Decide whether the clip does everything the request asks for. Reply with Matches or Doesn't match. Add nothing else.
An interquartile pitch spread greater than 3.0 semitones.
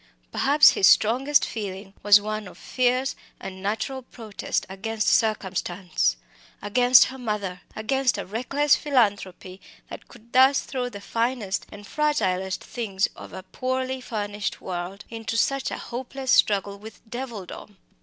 Matches